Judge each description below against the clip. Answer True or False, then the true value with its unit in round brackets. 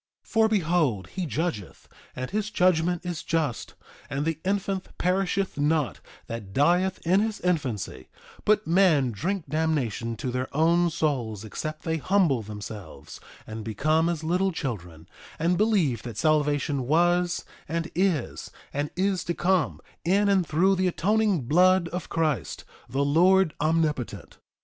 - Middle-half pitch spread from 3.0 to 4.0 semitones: False (5.3 semitones)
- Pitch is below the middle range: False (160 Hz)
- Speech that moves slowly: False (145 wpm)